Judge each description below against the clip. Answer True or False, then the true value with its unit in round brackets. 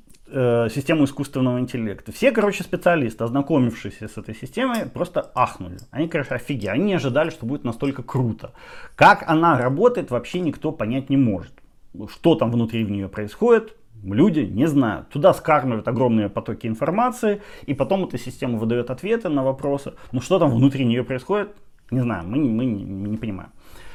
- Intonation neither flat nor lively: False (6.0 semitones)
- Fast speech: True (170 wpm)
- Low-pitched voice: True (130 Hz)